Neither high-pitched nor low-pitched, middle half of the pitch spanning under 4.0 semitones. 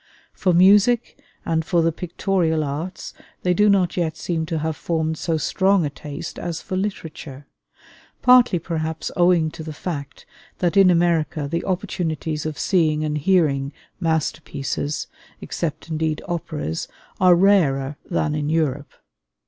Yes: medium, 165 Hz; average, 2.8 semitones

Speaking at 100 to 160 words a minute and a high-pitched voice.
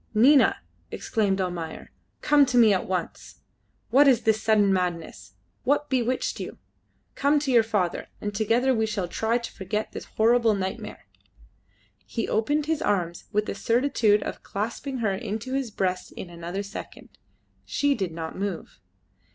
Yes: average, 155 wpm; high, 220 Hz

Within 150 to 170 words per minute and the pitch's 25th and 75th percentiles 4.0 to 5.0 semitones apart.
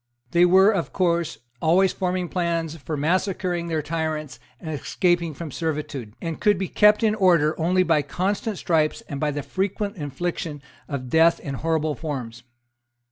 No: average, 160 wpm; average, 3.3 semitones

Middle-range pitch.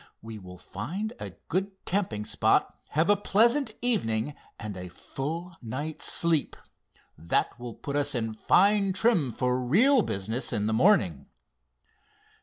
Yes: medium, 145 Hz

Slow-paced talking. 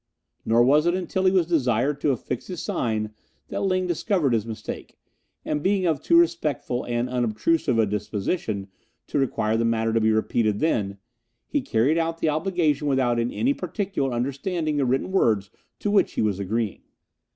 No: average, 175 wpm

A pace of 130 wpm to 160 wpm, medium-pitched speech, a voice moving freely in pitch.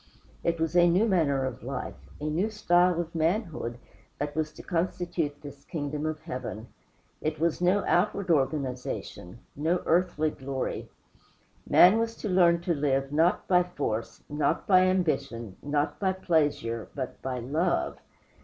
No: average, 150 wpm; medium, 155 Hz; average, 4.2 semitones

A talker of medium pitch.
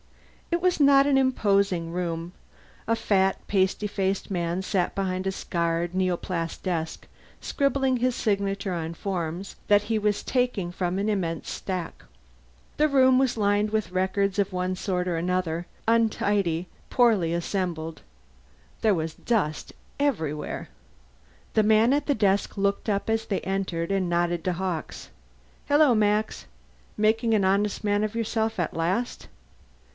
No: high, 195 Hz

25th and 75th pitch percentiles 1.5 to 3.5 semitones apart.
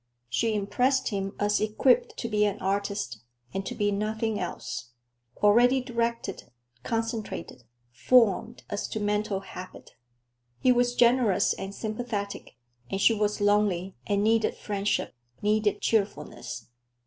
Yes: narrow, 2.4 semitones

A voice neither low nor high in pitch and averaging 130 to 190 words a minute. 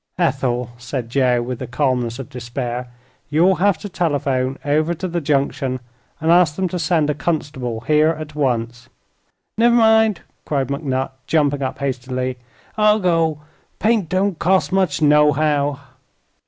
Yes: medium, 145 Hz; average, 145 wpm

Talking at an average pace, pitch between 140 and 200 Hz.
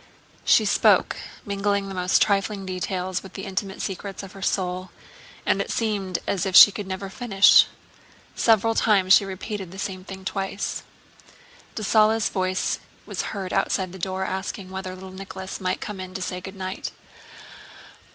Yes: average, 160 wpm; high, 190 Hz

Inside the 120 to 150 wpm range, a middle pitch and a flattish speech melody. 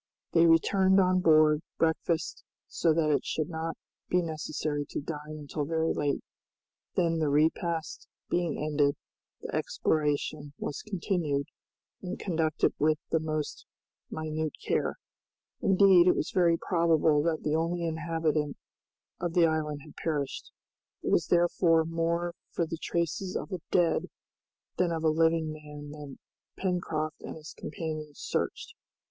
Yes: average, 140 wpm; medium, 160 Hz; narrow, 1.9 semitones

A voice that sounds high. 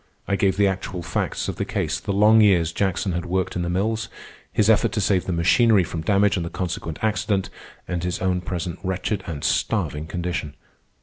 No: very low, 95 Hz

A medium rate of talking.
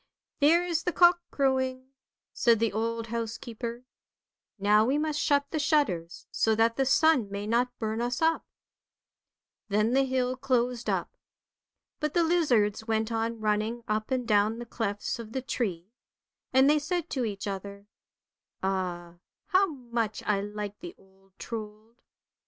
Yes: average, 165 wpm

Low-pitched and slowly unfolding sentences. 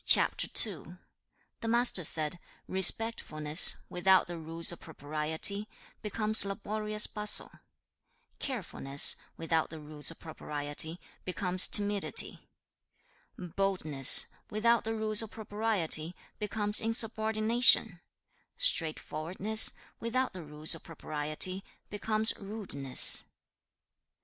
No: high, 190 Hz; slow, 90 wpm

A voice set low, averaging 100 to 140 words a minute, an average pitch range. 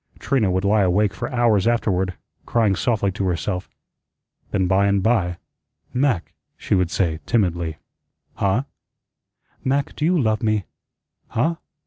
Yes: low, 100 Hz; slow, 135 wpm; average, 4.1 semitones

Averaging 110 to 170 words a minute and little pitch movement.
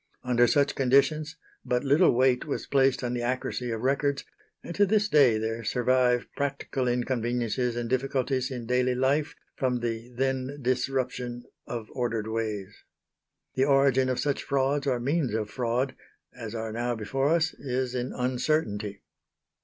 Yes: average, 155 wpm; narrow, 2.2 semitones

